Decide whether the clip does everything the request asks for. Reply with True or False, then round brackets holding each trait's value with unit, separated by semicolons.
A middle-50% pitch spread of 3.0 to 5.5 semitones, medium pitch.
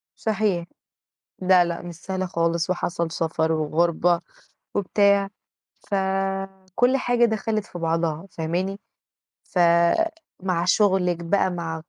False (2.5 semitones; 180 Hz)